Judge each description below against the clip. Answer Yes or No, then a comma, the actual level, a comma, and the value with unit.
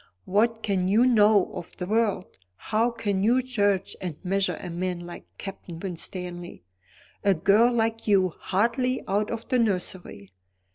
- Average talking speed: Yes, average, 150 wpm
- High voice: Yes, high, 200 Hz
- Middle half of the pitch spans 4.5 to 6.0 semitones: No, average, 3.8 semitones